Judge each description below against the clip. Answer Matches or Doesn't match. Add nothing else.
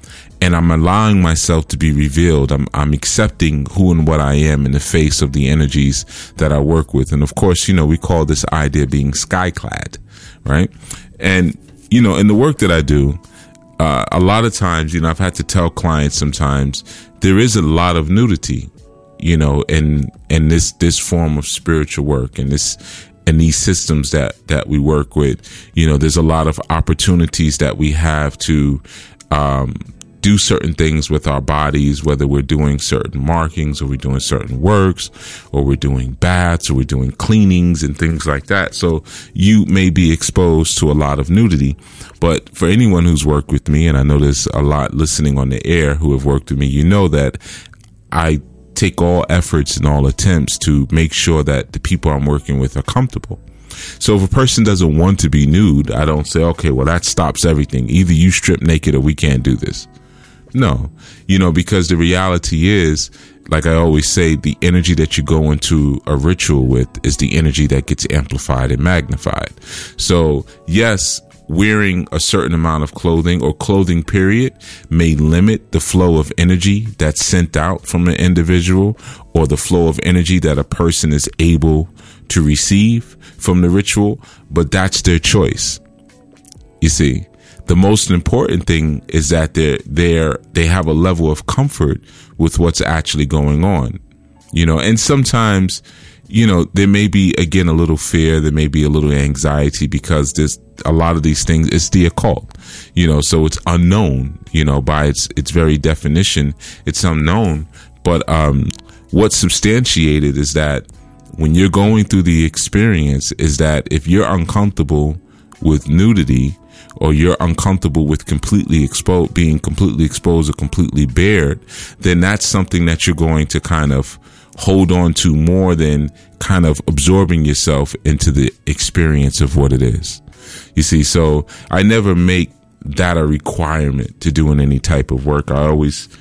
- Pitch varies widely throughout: Doesn't match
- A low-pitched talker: Matches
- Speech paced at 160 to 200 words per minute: Matches